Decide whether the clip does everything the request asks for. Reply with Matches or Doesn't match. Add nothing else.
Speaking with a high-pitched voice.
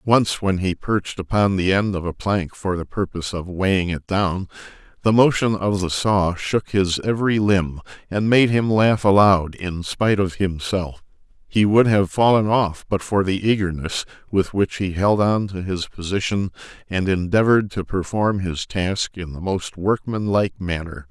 Doesn't match